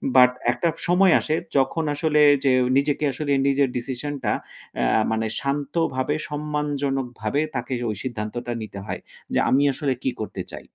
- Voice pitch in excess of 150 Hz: No, medium, 140 Hz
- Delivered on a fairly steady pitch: No, average, 3.0 semitones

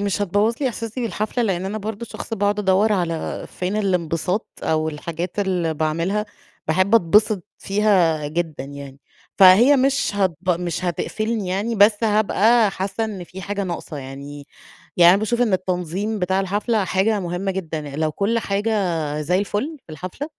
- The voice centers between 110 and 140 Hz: No, high, 190 Hz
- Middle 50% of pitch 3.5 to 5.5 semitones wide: Yes, average, 3.8 semitones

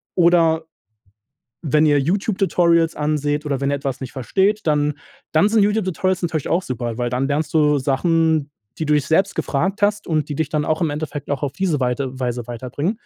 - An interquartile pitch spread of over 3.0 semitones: Yes, average, 3.7 semitones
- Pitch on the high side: No, medium, 155 Hz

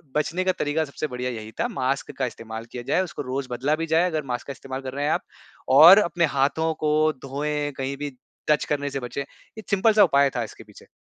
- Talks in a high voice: No, medium, 145 Hz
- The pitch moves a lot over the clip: No, average, 3.2 semitones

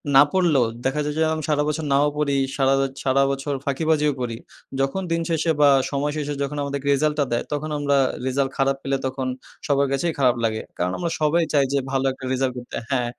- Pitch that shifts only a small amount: Yes, narrow, 2.0 semitones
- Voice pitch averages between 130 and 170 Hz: Yes, medium, 140 Hz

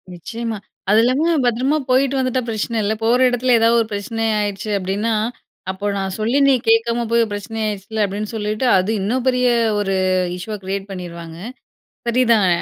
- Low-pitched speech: No, high, 225 Hz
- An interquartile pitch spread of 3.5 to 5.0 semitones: No, average, 3.0 semitones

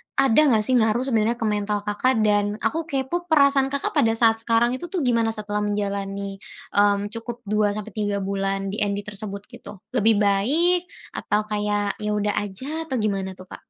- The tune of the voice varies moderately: Yes, average, 3.0 semitones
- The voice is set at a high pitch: Yes, high, 215 Hz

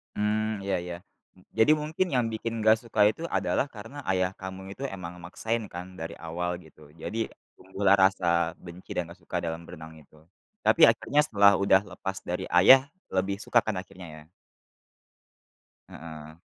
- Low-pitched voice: Yes, very low, 95 Hz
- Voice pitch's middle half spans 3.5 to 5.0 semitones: Yes, average, 4.1 semitones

